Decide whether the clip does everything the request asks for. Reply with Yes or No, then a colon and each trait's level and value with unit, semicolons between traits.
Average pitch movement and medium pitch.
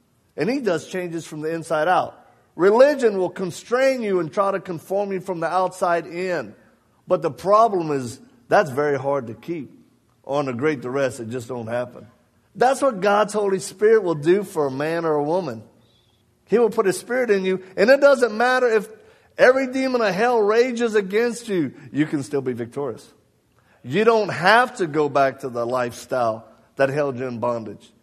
No: wide, 7.8 semitones; medium, 175 Hz